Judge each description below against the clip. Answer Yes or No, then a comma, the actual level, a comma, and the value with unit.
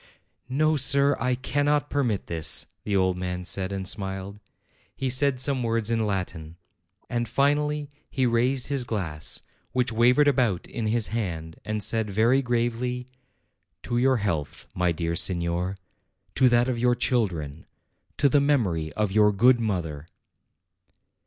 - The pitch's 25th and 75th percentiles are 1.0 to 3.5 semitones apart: No, wide, 5.4 semitones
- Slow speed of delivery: No, average, 145 wpm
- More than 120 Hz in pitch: No, low, 115 Hz